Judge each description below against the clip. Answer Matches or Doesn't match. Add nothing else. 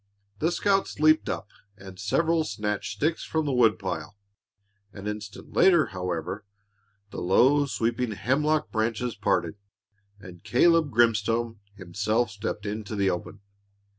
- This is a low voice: Matches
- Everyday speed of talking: Doesn't match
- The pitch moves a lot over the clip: Matches